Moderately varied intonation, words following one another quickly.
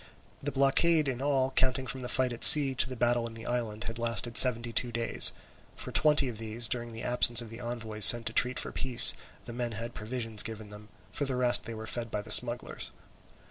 No: narrow, 2.1 semitones; fast, 225 wpm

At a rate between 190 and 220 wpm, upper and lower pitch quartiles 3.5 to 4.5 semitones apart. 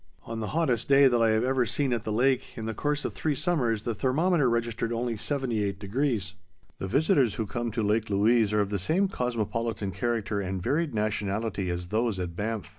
Yes: average, 200 wpm; average, 3.8 semitones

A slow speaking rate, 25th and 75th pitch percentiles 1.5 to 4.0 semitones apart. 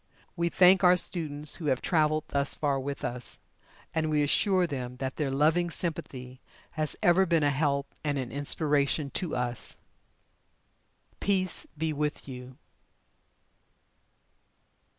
Yes: slow, 130 wpm; average, 3.5 semitones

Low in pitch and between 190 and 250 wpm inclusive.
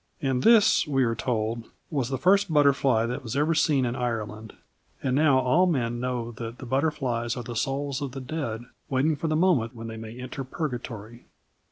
Yes: low, 130 Hz; average, 195 wpm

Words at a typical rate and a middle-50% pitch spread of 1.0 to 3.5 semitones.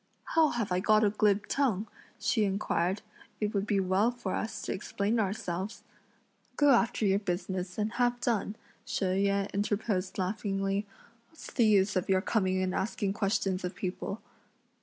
Yes: average, 160 wpm; narrow, 2.4 semitones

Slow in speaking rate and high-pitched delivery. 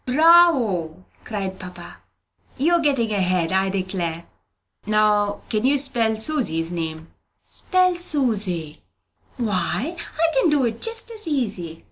Yes: slow, 120 wpm; high, 215 Hz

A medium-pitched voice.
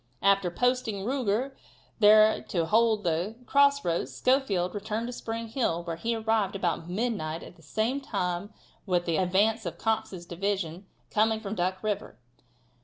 No: high, 205 Hz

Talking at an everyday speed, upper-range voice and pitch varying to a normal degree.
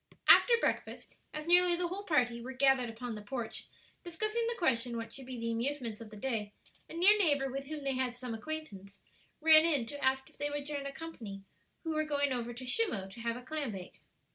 No: fast, 220 wpm; very high, 265 Hz; average, 5.0 semitones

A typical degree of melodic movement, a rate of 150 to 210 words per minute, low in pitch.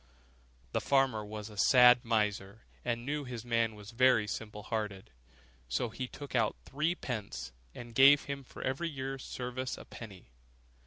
Yes: average, 3.6 semitones; average, 160 wpm; low, 120 Hz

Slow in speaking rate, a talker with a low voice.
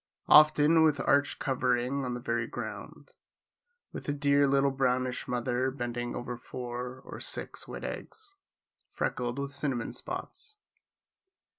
Yes: slow, 130 wpm; low, 130 Hz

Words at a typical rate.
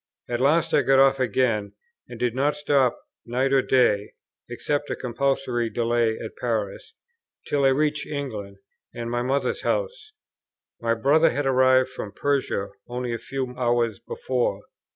Yes: average, 150 wpm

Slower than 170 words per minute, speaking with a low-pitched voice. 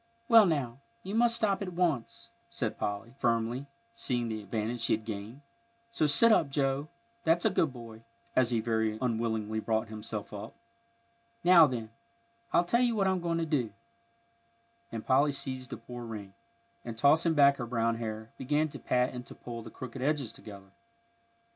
No: average, 175 wpm; low, 125 Hz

